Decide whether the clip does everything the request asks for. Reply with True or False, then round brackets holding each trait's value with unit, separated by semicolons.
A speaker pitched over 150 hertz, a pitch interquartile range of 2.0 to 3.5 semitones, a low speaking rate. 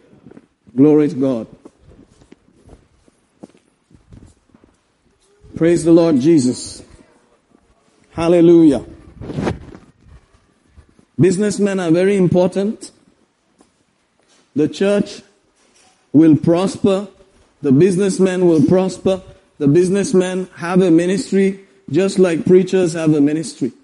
True (185 Hz; 2.7 semitones; 80 wpm)